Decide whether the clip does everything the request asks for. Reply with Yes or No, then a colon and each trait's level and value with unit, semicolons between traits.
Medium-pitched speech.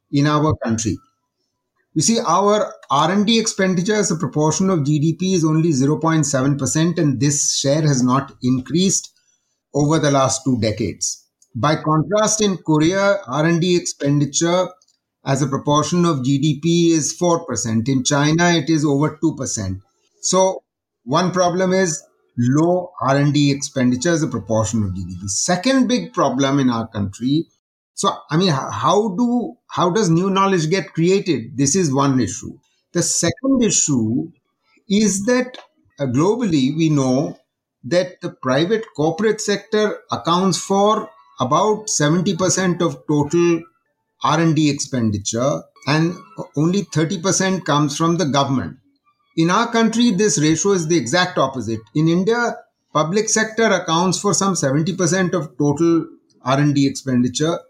Yes: medium, 160 Hz